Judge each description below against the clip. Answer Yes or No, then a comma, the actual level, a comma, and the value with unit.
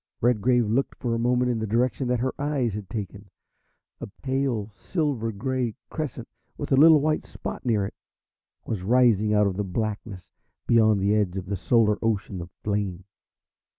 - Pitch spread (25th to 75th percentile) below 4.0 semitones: Yes, average, 3.6 semitones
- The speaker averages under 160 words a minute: No, average, 175 wpm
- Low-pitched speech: Yes, low, 115 Hz